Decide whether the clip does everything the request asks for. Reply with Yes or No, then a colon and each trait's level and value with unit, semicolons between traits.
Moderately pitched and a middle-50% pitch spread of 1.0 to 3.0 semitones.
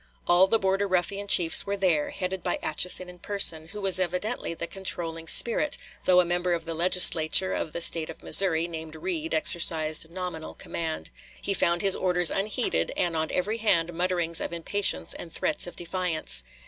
Yes: medium, 175 Hz; narrow, 2.5 semitones